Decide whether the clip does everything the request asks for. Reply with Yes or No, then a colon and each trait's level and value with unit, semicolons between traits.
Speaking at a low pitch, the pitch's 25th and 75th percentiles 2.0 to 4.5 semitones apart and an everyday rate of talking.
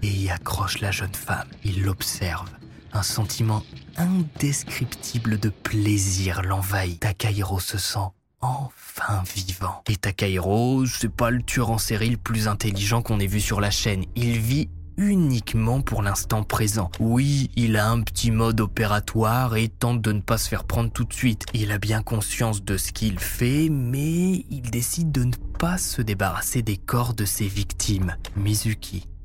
Yes: low, 110 Hz; average, 3.4 semitones; average, 170 wpm